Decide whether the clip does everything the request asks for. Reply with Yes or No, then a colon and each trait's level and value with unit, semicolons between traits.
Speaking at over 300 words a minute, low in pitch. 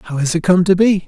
No: fast, 335 wpm; medium, 175 Hz